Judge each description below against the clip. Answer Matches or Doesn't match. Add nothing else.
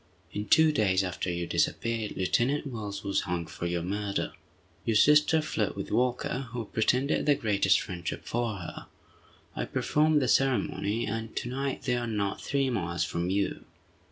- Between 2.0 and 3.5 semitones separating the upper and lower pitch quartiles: Doesn't match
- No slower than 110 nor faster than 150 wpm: Doesn't match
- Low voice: Matches